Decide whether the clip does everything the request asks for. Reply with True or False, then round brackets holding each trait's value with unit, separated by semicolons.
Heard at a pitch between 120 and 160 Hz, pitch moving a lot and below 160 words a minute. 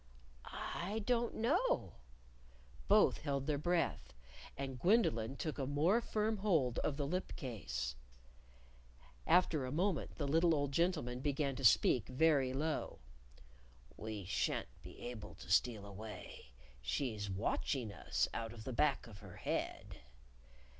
True (140 Hz; 6.5 semitones; 135 wpm)